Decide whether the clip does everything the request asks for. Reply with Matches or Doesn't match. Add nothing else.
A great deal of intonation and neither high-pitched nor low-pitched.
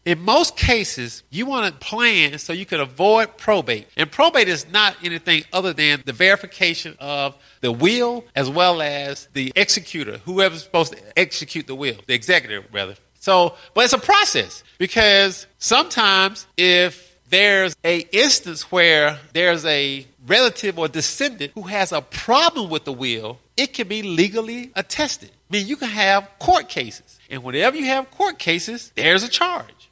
Matches